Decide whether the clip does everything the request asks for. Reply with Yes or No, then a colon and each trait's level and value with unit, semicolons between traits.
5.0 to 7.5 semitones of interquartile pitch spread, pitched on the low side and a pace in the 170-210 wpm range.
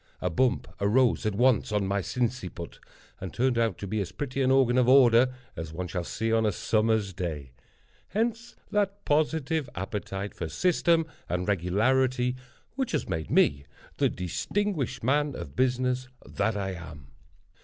No: wide, 5.6 semitones; low, 115 Hz; average, 160 wpm